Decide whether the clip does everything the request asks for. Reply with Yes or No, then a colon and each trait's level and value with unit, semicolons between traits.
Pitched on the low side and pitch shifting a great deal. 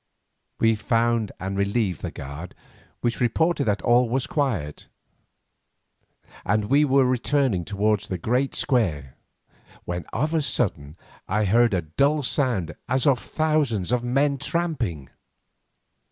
Yes: low, 120 Hz; wide, 6.1 semitones